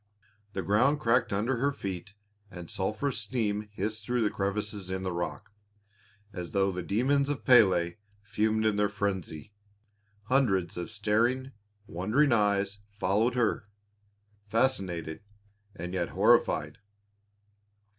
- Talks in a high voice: No, low, 105 Hz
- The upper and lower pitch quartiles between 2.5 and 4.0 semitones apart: Yes, average, 3.7 semitones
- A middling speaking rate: No, slow, 120 wpm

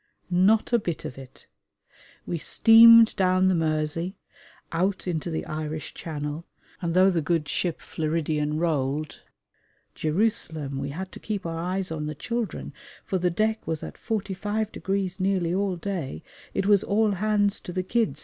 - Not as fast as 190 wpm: Yes, average, 160 wpm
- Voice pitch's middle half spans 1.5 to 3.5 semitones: No, average, 4.3 semitones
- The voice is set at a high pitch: No, medium, 180 Hz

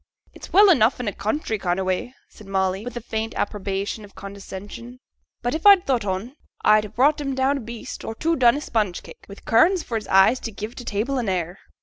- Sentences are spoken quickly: Yes, fast, 235 wpm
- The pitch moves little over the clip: No, average, 4.6 semitones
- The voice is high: Yes, high, 225 Hz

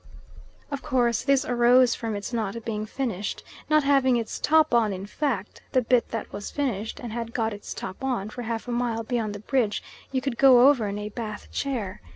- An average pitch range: Yes, average, 3.4 semitones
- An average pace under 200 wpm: No, fast, 205 wpm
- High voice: Yes, high, 235 Hz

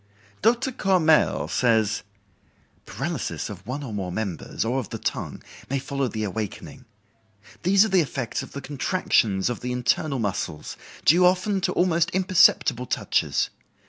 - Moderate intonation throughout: No, wide, 8.4 semitones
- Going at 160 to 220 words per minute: No, average, 145 wpm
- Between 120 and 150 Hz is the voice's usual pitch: Yes, low, 135 Hz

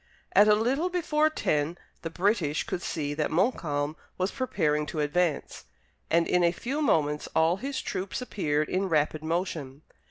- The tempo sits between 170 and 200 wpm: No, average, 160 wpm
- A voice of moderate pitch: Yes, medium, 170 Hz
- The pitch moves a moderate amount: No, wide, 5.7 semitones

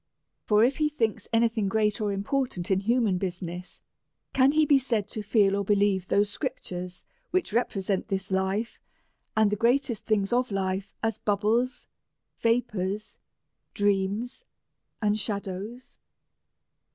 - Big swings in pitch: No, average, 3.3 semitones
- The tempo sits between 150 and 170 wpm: No, average, 140 wpm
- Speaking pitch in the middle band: No, high, 210 Hz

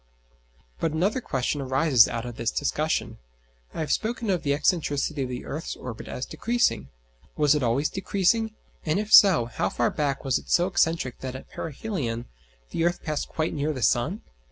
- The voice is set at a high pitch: No, medium, 150 Hz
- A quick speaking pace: No, average, 180 wpm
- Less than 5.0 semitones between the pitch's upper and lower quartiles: No, wide, 5.4 semitones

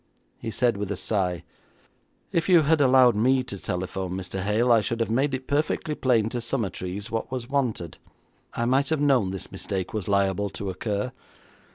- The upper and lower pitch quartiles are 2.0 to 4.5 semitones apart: No, average, 5.1 semitones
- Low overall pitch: Yes, low, 115 Hz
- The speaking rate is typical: Yes, average, 185 wpm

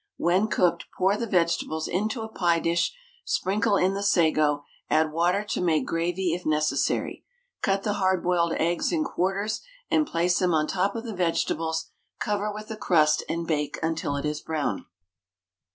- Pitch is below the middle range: No, medium, 175 Hz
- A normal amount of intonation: Yes, average, 3.7 semitones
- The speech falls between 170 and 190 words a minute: Yes, average, 175 wpm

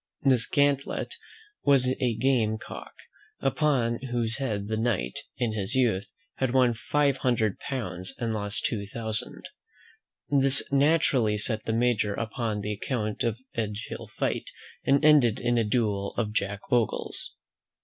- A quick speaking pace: No, average, 145 wpm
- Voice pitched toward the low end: Yes, low, 115 Hz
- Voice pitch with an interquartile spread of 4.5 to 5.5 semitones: No, average, 3.5 semitones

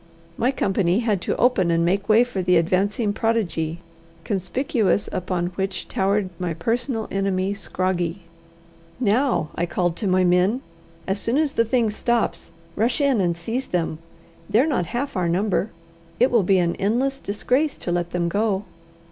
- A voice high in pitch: Yes, high, 200 Hz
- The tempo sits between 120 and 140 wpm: No, average, 165 wpm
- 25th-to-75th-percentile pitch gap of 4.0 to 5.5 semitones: Yes, average, 4.5 semitones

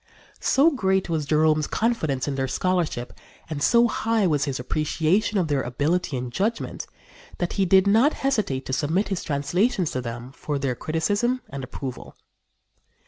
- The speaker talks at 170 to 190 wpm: No, average, 160 wpm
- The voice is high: No, medium, 160 Hz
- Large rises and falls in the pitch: Yes, wide, 6.5 semitones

